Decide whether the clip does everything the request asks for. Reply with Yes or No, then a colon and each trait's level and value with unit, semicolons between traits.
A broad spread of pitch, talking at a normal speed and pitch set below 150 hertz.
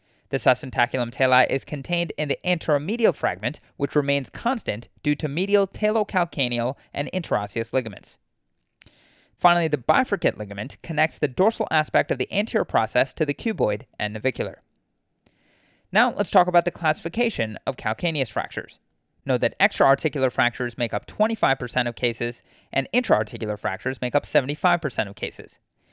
Yes: wide, 6.0 semitones; average, 145 wpm; medium, 140 Hz